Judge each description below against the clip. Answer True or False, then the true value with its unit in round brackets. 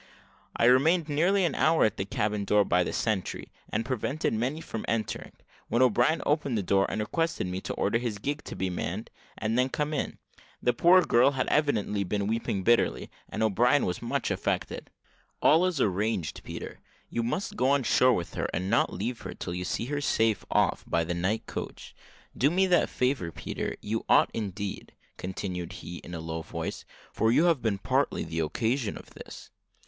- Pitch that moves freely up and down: True (6.4 semitones)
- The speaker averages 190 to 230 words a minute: True (195 wpm)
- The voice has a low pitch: True (115 Hz)